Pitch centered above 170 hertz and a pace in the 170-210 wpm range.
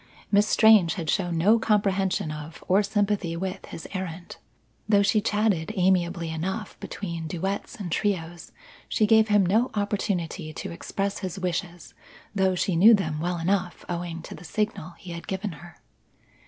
No: medium, 185 Hz; average, 160 wpm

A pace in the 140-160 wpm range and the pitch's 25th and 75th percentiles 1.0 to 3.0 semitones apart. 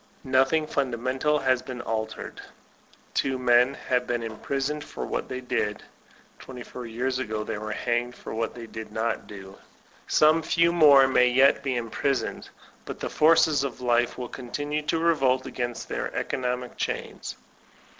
Yes: average, 155 wpm; narrow, 2.6 semitones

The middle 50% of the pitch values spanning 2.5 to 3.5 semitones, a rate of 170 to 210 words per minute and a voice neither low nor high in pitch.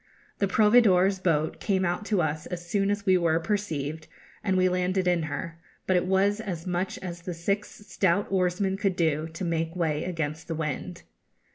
Yes: average, 2.9 semitones; average, 185 wpm; medium, 180 Hz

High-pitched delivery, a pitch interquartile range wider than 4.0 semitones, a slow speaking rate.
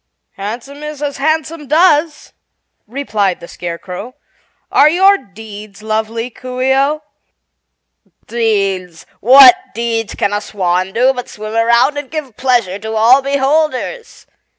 Yes: high, 240 Hz; average, 5.1 semitones; slow, 130 wpm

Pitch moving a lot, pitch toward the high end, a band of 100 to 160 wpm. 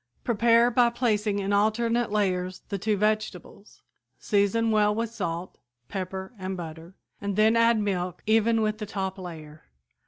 No: average, 3.0 semitones; high, 210 Hz; average, 150 wpm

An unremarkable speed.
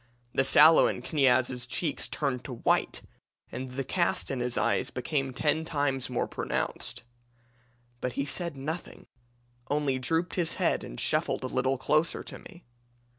Yes: average, 155 wpm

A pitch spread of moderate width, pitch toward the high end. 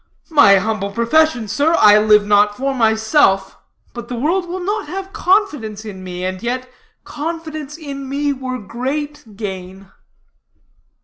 No: wide, 6.5 semitones; very high, 255 Hz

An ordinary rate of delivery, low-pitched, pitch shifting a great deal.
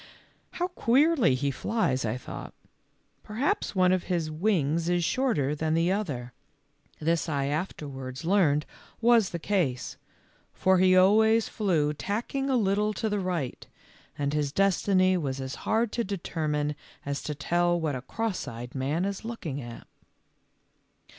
No: average, 150 wpm; medium, 175 Hz; wide, 6.3 semitones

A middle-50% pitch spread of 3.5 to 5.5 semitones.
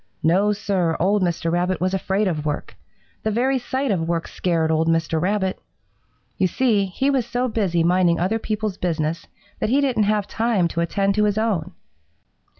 Yes: average, 4.2 semitones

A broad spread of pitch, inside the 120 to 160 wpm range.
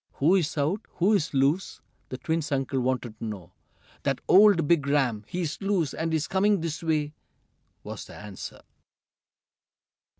No: average, 4.7 semitones; average, 140 wpm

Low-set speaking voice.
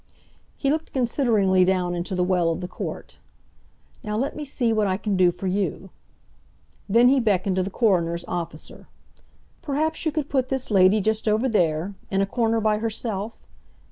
No: high, 210 Hz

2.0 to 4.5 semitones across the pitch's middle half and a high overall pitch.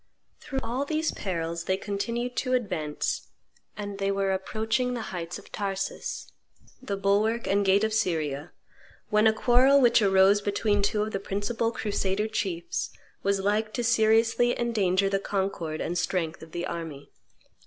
Yes: average, 3.0 semitones; high, 200 Hz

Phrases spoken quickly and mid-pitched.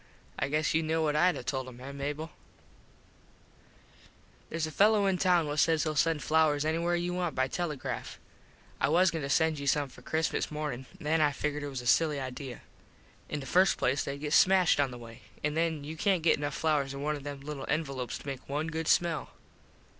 Yes: fast, 220 wpm; medium, 150 Hz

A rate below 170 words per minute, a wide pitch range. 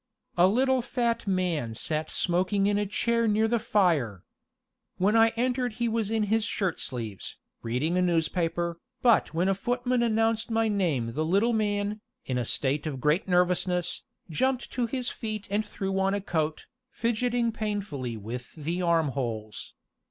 Yes: average, 160 wpm; wide, 6.1 semitones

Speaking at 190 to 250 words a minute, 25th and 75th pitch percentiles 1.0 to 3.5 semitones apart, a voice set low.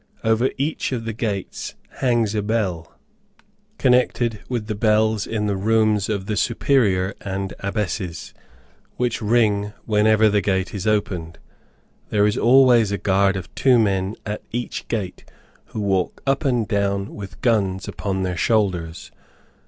No: average, 145 wpm; narrow, 2.6 semitones; low, 105 Hz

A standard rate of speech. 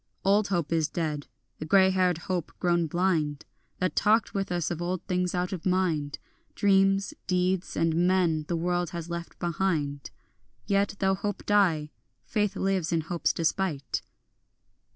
Yes: average, 150 wpm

